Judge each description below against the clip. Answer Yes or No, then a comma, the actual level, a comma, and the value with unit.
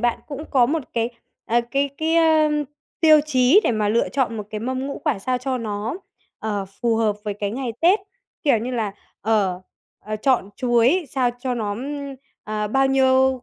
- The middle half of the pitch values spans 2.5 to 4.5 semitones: Yes, average, 4.1 semitones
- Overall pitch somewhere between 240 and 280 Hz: Yes, very high, 250 Hz